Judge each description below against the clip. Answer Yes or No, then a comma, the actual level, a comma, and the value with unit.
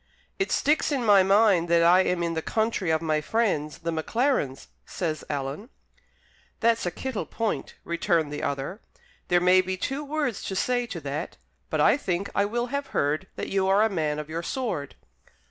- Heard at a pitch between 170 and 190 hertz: Yes, medium, 185 Hz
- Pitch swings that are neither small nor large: No, wide, 6.1 semitones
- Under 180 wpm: No, average, 190 wpm